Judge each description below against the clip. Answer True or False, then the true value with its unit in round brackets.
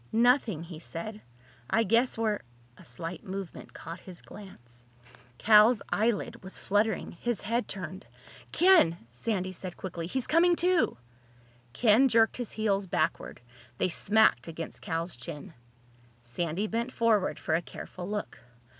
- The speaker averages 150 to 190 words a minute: False (135 wpm)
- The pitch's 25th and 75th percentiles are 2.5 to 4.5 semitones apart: False (5.2 semitones)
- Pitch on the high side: True (200 Hz)